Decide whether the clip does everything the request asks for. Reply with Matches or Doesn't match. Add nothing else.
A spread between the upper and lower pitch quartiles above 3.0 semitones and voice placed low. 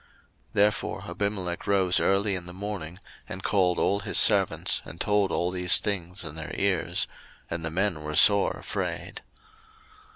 Doesn't match